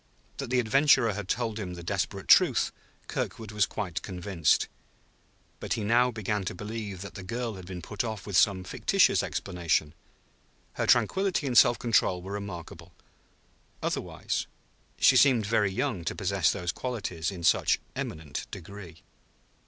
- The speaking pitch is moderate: No, low, 100 Hz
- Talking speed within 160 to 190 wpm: No, average, 150 wpm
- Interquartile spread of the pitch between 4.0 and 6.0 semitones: Yes, average, 4.3 semitones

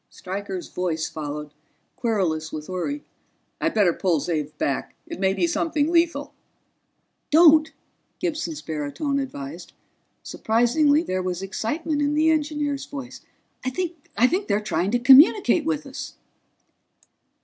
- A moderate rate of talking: No, slow, 125 wpm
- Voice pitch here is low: No, high, 245 Hz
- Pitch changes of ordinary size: No, wide, 9.0 semitones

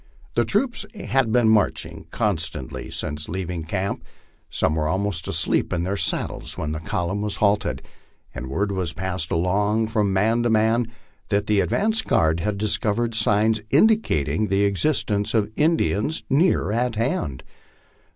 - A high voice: No, low, 105 Hz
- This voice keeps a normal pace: Yes, average, 150 wpm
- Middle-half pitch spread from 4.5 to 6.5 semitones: No, average, 3.9 semitones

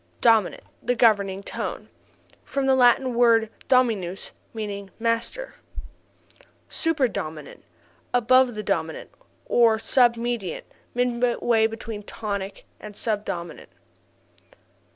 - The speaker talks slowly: Yes, slow, 110 wpm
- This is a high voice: Yes, high, 225 Hz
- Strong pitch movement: No, average, 3.4 semitones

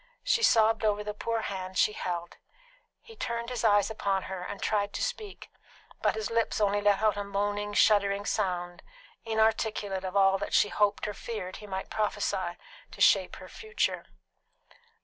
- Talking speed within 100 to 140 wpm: No, average, 170 wpm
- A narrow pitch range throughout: Yes, narrow, 2.0 semitones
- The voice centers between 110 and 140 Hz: No, high, 205 Hz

